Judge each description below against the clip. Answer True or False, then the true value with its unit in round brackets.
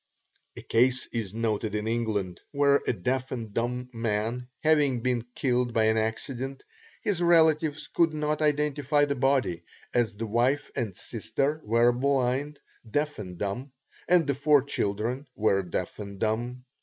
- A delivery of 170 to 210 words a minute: False (155 wpm)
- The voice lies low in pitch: True (125 Hz)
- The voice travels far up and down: False (4.4 semitones)